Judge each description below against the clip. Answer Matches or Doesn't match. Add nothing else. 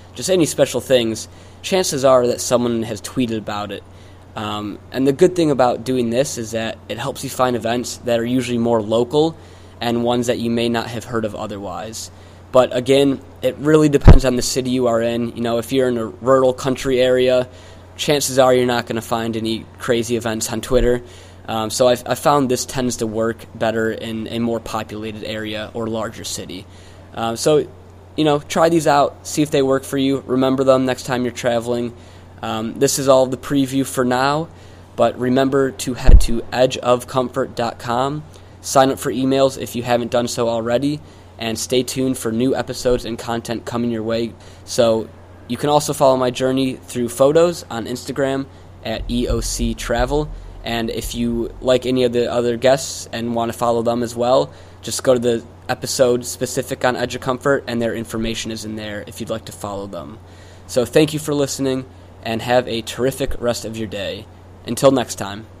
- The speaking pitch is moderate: Doesn't match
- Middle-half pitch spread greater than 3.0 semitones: Doesn't match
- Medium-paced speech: Matches